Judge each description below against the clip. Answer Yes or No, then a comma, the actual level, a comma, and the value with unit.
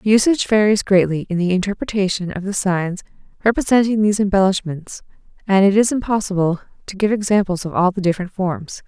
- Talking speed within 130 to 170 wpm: Yes, average, 160 wpm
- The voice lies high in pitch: Yes, high, 195 Hz